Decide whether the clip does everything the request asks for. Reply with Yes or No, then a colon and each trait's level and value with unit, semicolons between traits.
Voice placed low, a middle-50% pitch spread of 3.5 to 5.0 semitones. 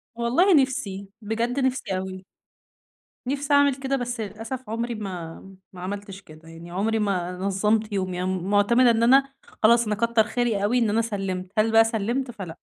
No: high, 220 Hz; average, 3.9 semitones